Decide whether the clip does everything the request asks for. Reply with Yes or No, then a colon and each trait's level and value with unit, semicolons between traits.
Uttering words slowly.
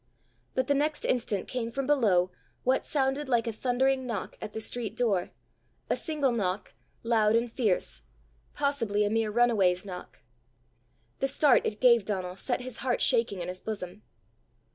No: average, 165 wpm